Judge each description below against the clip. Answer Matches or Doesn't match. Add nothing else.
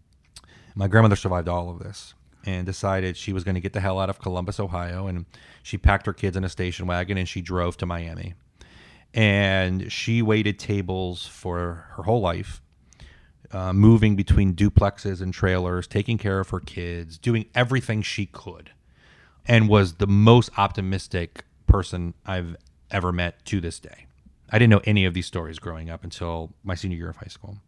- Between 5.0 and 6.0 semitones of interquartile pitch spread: Doesn't match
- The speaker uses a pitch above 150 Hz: Doesn't match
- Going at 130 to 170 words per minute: Doesn't match